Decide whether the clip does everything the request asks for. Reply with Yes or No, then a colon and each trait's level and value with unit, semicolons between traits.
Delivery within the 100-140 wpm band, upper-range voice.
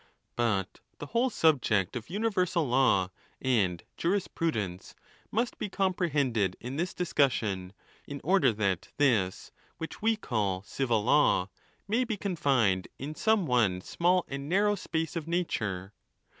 No: slow, 135 wpm; medium, 140 Hz